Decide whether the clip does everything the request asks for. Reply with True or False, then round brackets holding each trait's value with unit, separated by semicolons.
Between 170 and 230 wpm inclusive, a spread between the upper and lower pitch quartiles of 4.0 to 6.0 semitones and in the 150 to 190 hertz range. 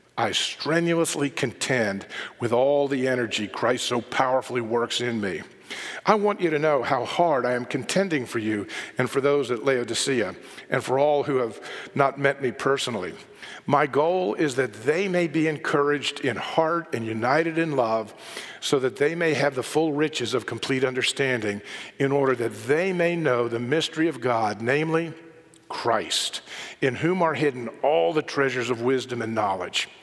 False (175 wpm; 4.3 semitones; 140 Hz)